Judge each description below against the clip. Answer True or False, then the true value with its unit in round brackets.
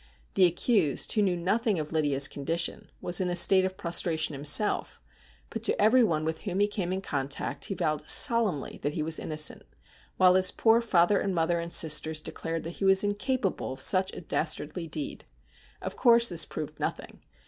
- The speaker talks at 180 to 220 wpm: True (190 wpm)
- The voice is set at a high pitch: False (175 Hz)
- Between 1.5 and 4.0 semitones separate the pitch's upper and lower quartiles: False (4.4 semitones)